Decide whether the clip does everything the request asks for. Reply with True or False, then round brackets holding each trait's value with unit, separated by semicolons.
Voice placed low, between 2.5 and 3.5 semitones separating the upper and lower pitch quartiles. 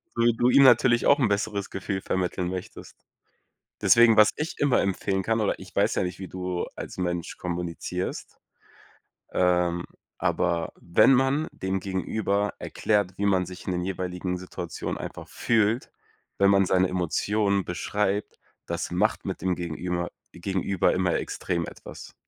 True (95 Hz; 2.8 semitones)